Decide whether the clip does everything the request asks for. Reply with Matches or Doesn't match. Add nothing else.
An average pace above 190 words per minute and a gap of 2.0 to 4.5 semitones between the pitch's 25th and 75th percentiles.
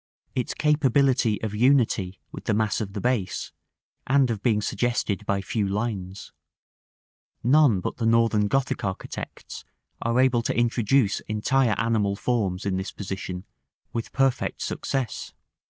Doesn't match